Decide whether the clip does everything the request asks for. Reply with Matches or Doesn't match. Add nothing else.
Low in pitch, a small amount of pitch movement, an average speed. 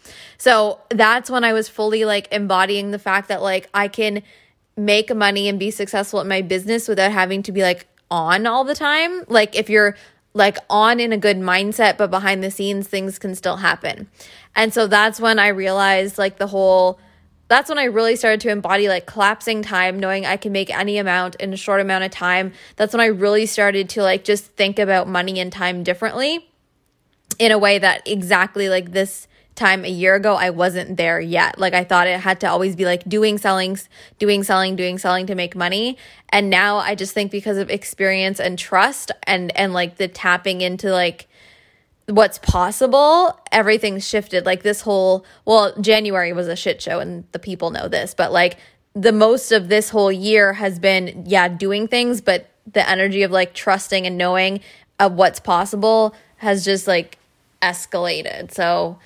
Doesn't match